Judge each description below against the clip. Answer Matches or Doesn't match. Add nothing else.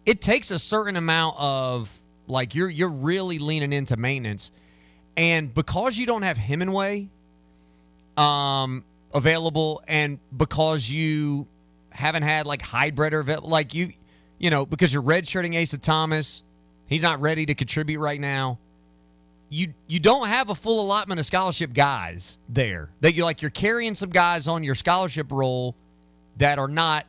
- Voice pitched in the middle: Matches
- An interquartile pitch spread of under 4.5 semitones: Doesn't match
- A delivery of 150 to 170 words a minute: Matches